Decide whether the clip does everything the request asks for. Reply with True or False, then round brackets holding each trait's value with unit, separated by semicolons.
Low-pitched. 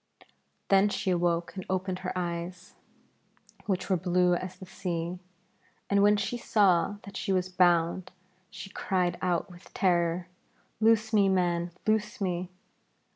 False (185 Hz)